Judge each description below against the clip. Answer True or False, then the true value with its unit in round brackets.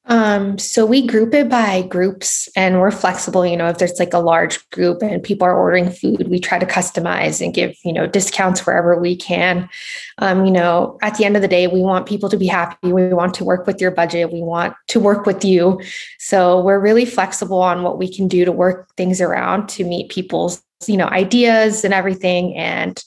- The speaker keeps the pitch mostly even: True (2.0 semitones)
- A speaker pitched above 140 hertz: True (185 Hz)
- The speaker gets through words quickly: True (220 wpm)